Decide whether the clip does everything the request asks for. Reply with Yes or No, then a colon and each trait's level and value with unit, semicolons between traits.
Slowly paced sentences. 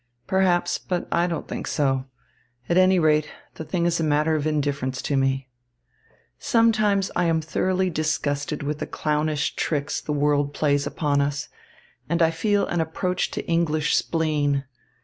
No: average, 160 wpm